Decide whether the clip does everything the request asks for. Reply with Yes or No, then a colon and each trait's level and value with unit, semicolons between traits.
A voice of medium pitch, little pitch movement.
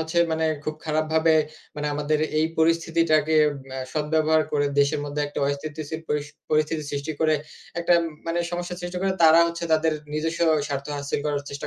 Yes: medium, 155 Hz; narrow, 1.5 semitones